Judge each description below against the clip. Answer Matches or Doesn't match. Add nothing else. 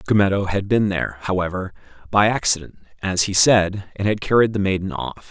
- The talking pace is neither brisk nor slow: Matches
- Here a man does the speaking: Matches